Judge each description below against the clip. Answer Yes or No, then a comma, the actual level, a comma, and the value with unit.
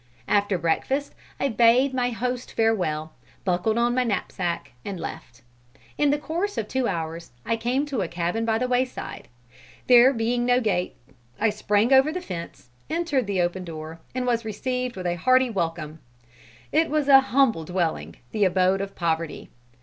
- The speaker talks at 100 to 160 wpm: No, average, 170 wpm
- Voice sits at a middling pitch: No, high, 225 Hz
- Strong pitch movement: Yes, wide, 6.2 semitones